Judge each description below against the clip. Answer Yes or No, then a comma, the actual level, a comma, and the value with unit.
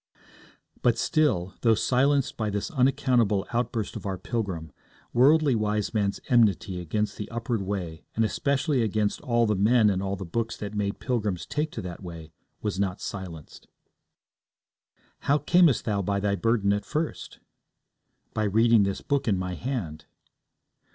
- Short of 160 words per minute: Yes, average, 150 wpm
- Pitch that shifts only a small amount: No, average, 4.0 semitones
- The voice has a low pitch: Yes, low, 105 Hz